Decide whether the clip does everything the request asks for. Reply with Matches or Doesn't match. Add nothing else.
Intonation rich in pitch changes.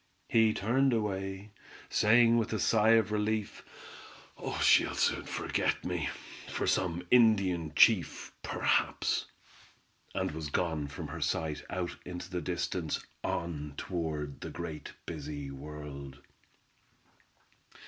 Matches